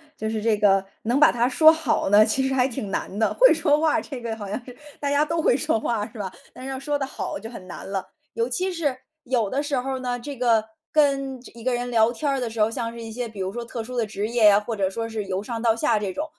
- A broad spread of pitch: No, average, 3.7 semitones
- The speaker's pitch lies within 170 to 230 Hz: No, high, 240 Hz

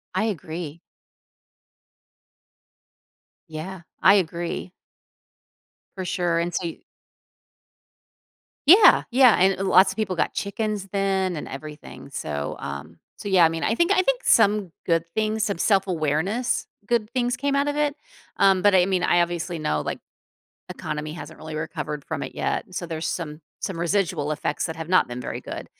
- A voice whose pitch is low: No, medium, 180 Hz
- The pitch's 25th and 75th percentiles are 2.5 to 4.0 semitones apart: No, average, 4.4 semitones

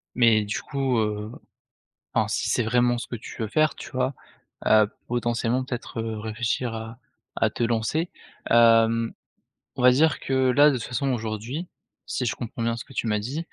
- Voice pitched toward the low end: Yes, low, 120 Hz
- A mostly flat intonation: Yes, narrow, 2.3 semitones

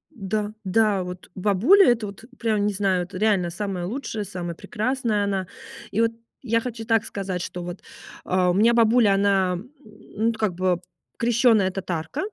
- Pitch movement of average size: Yes, average, 3.4 semitones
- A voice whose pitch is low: No, high, 205 Hz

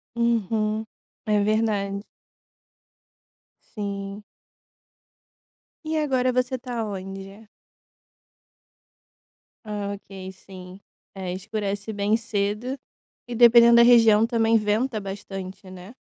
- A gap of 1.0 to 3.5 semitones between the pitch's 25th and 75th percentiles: Yes, average, 2.9 semitones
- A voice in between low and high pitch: No, high, 210 Hz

